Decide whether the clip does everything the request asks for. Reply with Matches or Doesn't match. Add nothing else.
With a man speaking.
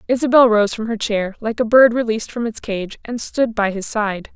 Doesn't match